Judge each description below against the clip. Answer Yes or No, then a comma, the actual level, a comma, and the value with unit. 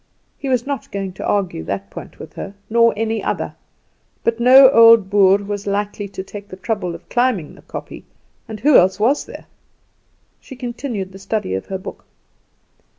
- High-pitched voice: Yes, high, 205 Hz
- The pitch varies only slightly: No, average, 3.6 semitones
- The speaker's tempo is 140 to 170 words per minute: No, average, 180 wpm